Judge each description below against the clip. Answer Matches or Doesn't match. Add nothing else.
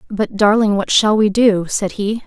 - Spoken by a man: Doesn't match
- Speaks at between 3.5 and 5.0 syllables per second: Matches